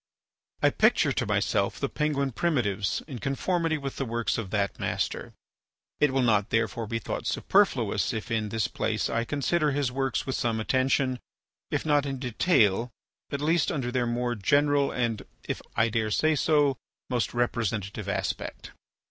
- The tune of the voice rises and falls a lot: No, average, 4.0 semitones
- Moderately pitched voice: No, low, 125 Hz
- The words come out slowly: No, average, 165 wpm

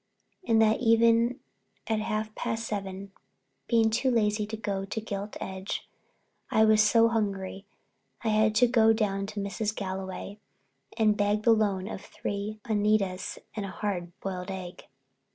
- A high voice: Yes, high, 210 Hz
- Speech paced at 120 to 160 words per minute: Yes, average, 155 wpm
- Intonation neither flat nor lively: No, narrow, 2.0 semitones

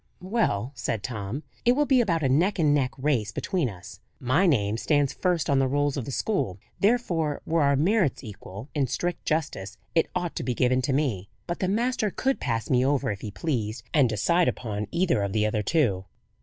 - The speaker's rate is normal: No, fast, 210 wpm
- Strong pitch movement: Yes, wide, 7.6 semitones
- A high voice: No, medium, 140 Hz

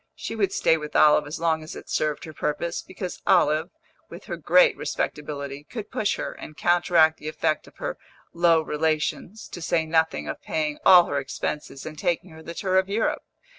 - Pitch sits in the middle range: Yes, medium, 160 Hz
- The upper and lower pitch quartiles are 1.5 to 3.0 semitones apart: Yes, narrow, 2.6 semitones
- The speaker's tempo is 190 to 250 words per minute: Yes, average, 195 wpm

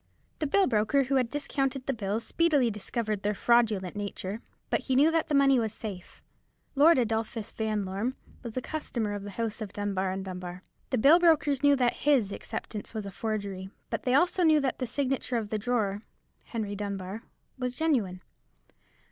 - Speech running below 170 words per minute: No, average, 180 wpm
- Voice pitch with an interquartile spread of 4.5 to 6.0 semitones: Yes, average, 5.0 semitones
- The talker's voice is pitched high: Yes, high, 230 Hz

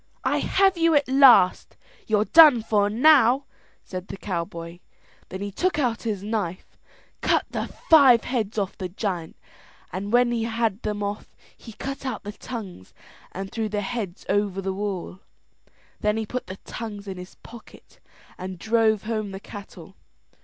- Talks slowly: No, average, 165 wpm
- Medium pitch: No, high, 210 Hz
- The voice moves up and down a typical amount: Yes, average, 3.6 semitones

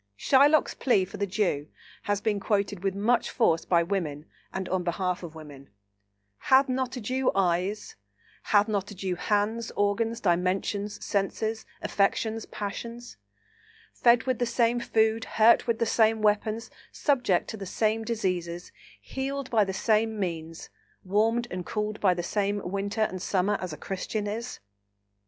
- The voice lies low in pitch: No, high, 205 Hz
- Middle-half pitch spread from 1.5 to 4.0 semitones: Yes, average, 3.4 semitones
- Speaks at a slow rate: No, average, 155 wpm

